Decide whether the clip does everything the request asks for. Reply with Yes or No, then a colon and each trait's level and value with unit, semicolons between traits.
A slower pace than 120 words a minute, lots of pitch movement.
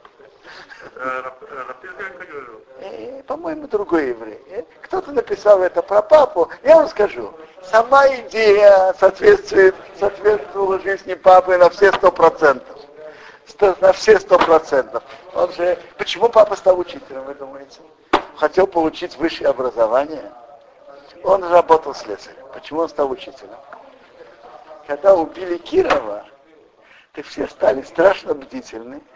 Yes: slow, 110 wpm; wide, 6.0 semitones